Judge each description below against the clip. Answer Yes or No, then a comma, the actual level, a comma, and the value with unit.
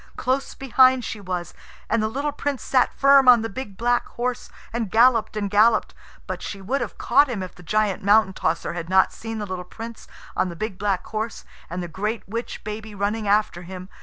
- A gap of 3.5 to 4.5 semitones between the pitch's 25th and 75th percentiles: Yes, average, 3.9 semitones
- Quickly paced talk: Yes, fast, 210 wpm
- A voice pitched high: Yes, high, 215 Hz